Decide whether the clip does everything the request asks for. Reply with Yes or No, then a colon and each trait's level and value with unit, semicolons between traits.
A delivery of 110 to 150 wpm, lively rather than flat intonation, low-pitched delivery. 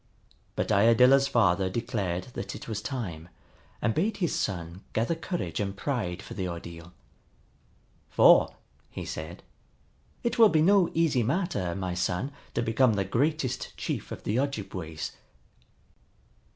Yes: average, 140 wpm; wide, 7.3 semitones; low, 110 Hz